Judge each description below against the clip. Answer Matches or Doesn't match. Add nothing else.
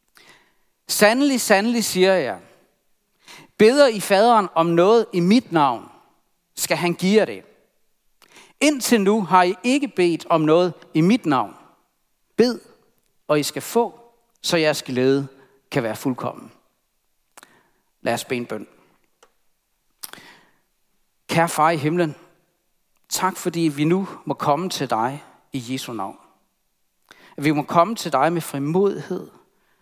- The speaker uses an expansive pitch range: Matches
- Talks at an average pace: Doesn't match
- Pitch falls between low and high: Matches